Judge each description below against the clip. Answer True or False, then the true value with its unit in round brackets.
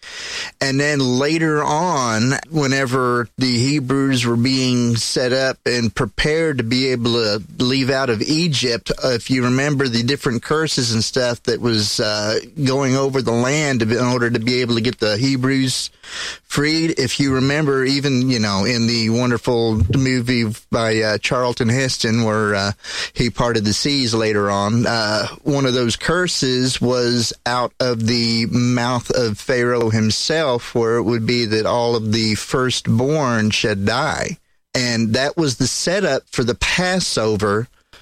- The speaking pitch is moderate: False (125 Hz)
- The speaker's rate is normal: True (160 wpm)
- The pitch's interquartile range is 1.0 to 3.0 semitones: True (2.7 semitones)